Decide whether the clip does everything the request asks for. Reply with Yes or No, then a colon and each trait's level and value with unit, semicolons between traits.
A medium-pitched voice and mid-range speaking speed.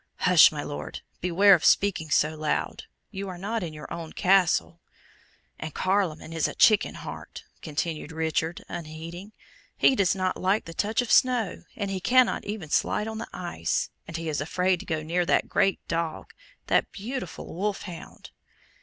Yes: medium, 180 Hz; average, 170 wpm